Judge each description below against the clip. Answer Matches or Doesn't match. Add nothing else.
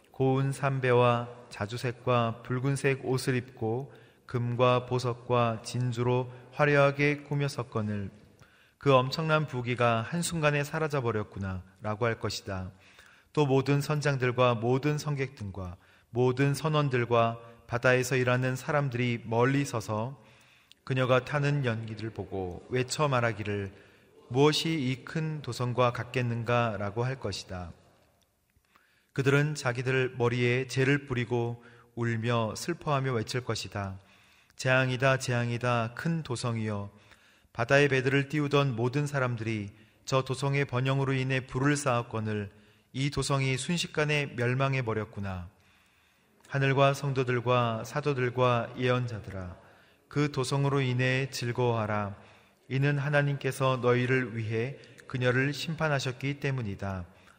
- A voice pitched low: Matches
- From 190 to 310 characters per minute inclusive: Matches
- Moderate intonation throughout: Matches